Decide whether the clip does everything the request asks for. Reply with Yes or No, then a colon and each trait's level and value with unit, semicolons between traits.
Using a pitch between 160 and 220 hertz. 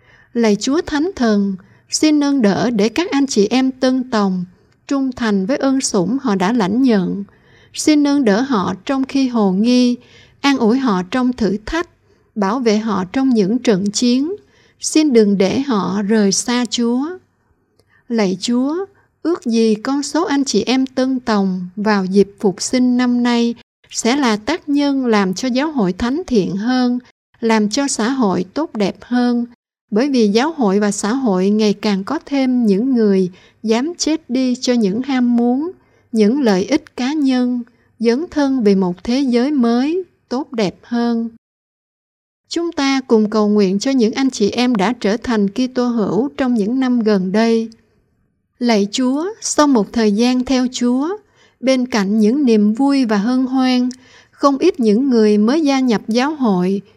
No: high, 240 Hz